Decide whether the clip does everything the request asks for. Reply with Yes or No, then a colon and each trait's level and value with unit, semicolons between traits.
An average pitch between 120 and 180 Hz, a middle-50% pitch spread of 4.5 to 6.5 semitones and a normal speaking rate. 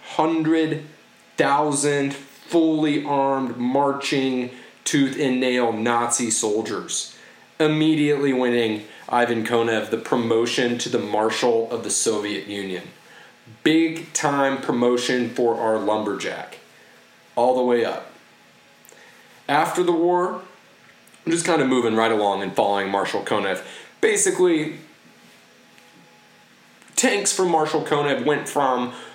No: low, 135 Hz; average, 4.8 semitones; slow, 110 wpm